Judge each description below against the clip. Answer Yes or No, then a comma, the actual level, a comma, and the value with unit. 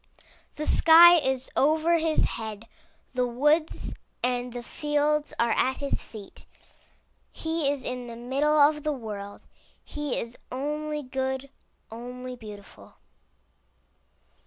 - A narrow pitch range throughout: No, average, 3.6 semitones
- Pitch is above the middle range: Yes, very high, 265 Hz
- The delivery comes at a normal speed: No, slow, 120 wpm